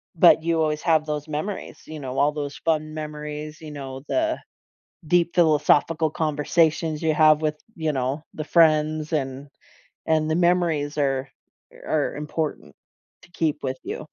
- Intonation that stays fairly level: Yes, narrow, 1.4 semitones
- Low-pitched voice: No, medium, 155 Hz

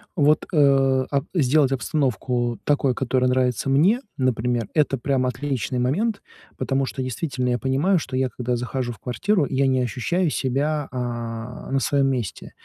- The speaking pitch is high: No, low, 130 Hz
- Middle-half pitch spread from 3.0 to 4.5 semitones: No, narrow, 2.5 semitones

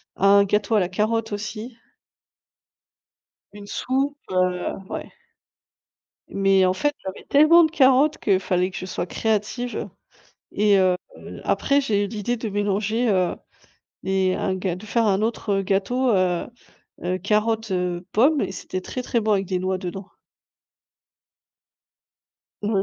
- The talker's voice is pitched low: No, high, 205 Hz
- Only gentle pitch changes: No, average, 3.5 semitones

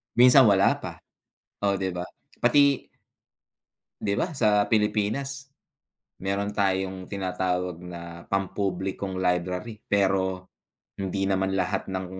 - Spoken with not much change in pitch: Yes, narrow, 1.9 semitones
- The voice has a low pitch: Yes, very low, 95 Hz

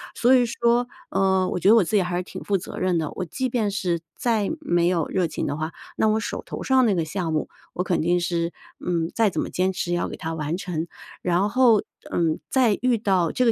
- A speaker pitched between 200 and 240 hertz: No, medium, 185 Hz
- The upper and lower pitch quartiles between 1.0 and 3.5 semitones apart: No, average, 4.5 semitones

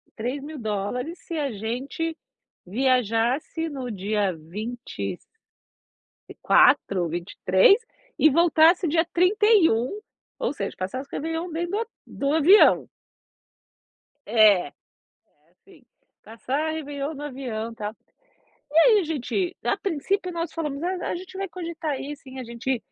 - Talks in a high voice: Yes, very high, 280 Hz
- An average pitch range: No, wide, 6.6 semitones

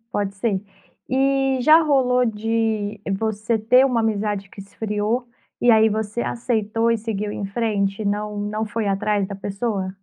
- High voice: Yes, high, 215 Hz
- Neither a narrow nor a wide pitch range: No, narrow, 2.3 semitones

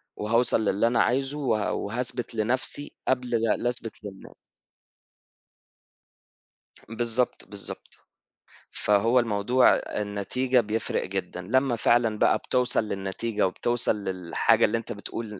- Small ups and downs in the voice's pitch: No, average, 3.1 semitones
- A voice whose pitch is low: Yes, low, 115 Hz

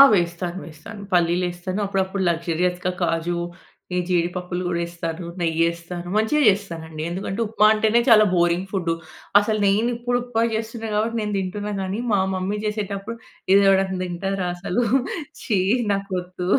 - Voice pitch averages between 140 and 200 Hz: Yes, medium, 185 Hz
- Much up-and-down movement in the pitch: No, average, 3.2 semitones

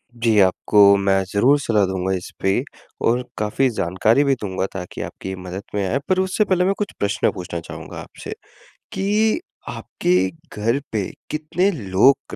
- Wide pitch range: Yes, wide, 6.8 semitones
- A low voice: Yes, low, 105 Hz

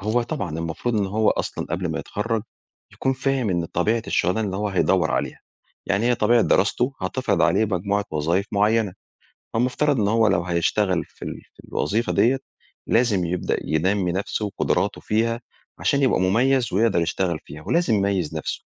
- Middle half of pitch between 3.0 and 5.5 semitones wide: Yes, average, 4.0 semitones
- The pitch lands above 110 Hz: No, low, 105 Hz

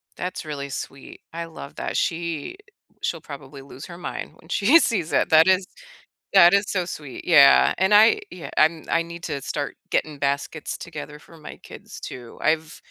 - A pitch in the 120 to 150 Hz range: No, medium, 160 Hz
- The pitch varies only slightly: No, average, 3.5 semitones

